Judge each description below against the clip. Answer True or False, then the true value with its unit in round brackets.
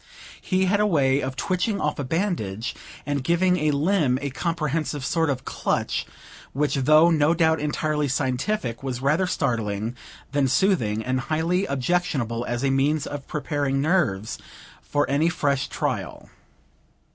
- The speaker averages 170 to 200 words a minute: False (145 wpm)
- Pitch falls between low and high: True (145 Hz)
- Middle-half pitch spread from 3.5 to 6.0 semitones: True (4.1 semitones)